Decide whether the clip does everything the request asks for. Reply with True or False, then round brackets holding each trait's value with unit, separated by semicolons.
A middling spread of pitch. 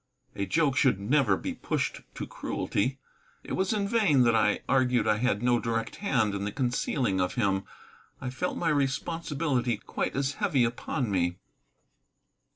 True (5.0 semitones)